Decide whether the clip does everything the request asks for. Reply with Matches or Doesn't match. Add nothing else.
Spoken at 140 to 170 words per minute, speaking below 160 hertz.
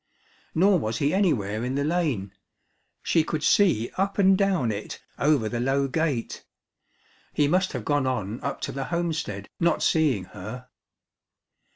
Matches